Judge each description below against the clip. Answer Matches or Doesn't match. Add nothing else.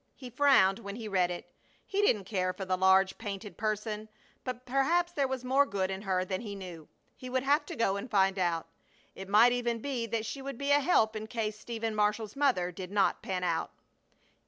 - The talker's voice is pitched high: Matches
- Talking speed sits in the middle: Doesn't match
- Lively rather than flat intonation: Doesn't match